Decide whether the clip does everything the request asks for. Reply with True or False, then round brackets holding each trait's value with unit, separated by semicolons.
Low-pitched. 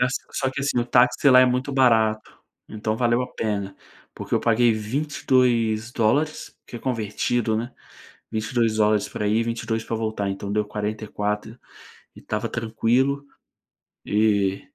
True (115 Hz)